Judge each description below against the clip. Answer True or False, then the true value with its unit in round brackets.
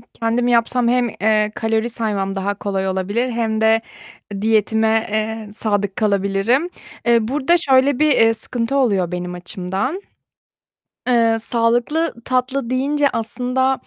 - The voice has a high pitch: True (225 Hz)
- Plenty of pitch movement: False (3.4 semitones)